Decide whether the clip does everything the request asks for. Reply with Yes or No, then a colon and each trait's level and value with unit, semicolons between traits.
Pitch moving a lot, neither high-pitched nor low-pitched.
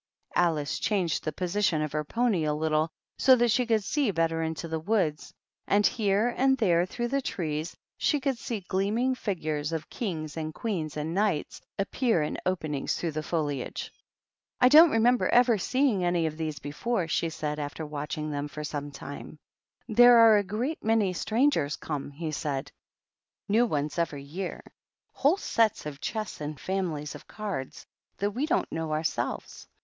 Yes: wide, 6.6 semitones; medium, 175 Hz